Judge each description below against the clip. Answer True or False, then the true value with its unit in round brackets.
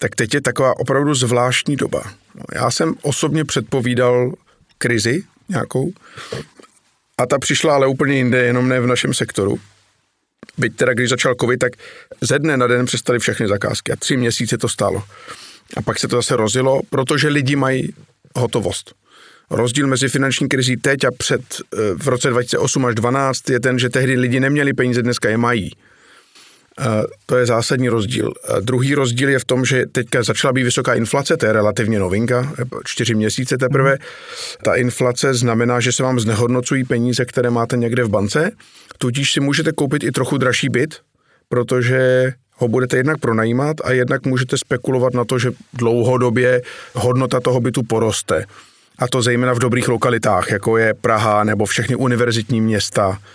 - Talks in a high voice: False (125 Hz)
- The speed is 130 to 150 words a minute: False (165 wpm)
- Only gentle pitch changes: True (1.9 semitones)